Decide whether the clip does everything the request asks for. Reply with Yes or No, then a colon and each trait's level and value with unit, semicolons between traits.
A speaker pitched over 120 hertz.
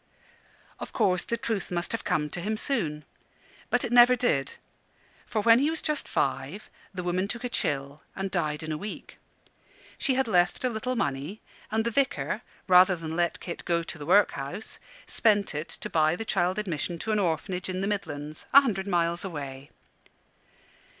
Yes: medium, 185 Hz